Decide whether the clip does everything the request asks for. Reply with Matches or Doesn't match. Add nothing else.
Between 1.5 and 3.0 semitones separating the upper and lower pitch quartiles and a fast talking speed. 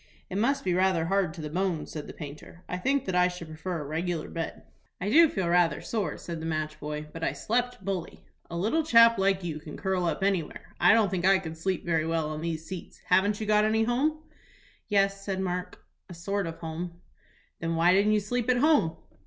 Doesn't match